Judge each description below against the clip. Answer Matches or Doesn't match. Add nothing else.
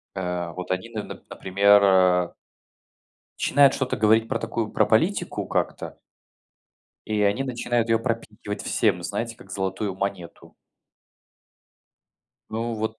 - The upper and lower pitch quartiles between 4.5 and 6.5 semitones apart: Doesn't match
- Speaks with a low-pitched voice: Matches